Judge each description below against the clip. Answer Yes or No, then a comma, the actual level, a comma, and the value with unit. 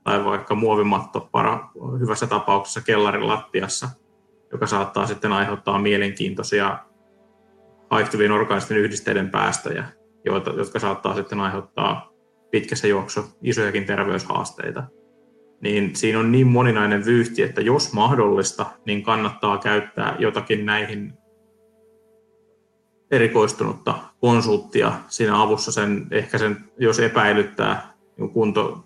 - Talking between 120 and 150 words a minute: No, average, 100 wpm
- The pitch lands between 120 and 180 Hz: No, low, 110 Hz